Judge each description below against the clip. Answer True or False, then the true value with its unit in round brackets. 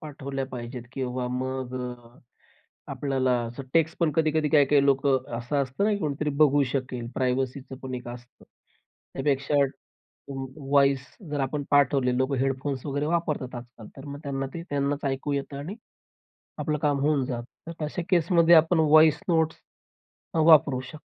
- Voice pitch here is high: False (140 Hz)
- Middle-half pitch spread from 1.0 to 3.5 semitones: True (2.6 semitones)